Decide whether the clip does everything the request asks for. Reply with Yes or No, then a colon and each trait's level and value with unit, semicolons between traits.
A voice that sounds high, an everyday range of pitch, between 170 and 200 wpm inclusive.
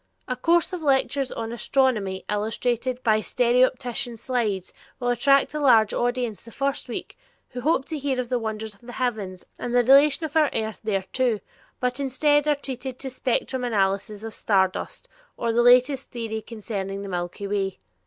Yes: high, 245 Hz; average, 3.5 semitones; average, 175 wpm